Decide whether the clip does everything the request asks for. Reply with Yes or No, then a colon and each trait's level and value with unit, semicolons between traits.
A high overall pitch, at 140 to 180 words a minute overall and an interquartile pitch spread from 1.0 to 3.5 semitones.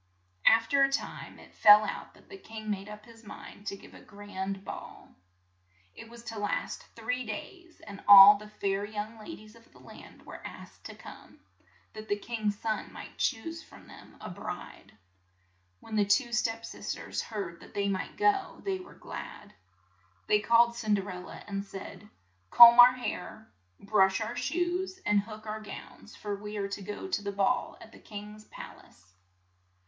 No: high, 215 Hz; average, 190 wpm; narrow, 2.5 semitones